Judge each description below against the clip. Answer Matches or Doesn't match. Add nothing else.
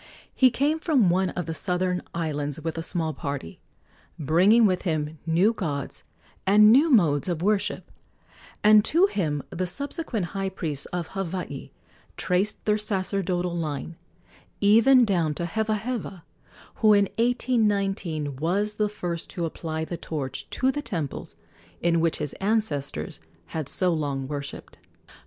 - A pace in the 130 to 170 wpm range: Matches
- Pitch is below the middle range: Doesn't match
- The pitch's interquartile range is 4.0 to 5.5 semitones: Matches